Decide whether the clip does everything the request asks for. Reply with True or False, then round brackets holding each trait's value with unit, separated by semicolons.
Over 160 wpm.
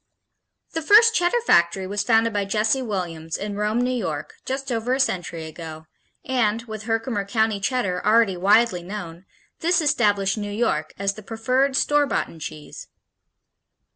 False (155 wpm)